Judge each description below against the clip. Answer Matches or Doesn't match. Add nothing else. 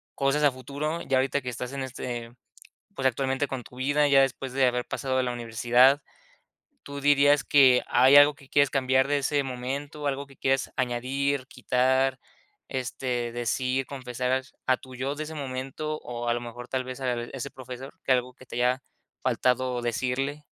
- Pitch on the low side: Matches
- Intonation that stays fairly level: Matches